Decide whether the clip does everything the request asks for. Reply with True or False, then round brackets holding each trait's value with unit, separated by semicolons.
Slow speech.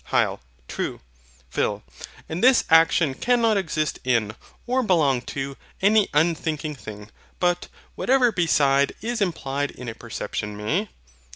True (125 wpm)